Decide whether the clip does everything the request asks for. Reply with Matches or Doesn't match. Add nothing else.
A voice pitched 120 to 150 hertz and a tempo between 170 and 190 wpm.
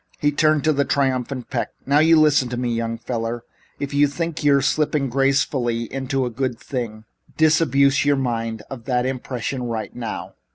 Matches